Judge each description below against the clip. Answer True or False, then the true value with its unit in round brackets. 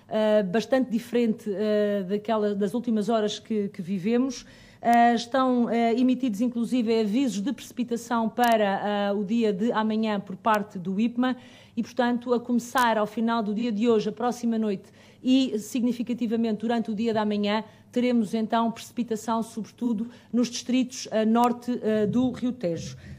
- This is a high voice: True (230 Hz)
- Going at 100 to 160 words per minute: True (155 wpm)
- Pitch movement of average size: False (2.1 semitones)